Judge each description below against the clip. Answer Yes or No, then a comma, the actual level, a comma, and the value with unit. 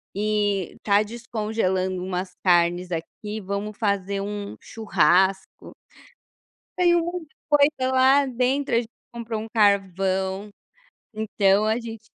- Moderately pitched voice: No, high, 210 Hz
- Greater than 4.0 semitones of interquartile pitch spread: No, average, 3.4 semitones